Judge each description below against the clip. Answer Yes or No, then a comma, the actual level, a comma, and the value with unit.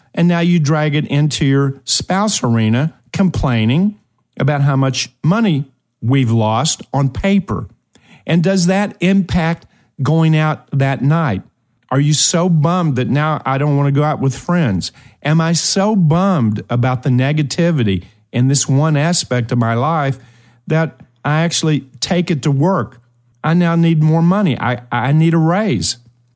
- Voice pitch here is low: No, medium, 145 Hz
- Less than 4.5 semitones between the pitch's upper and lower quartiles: No, average, 4.9 semitones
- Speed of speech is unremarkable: Yes, average, 160 wpm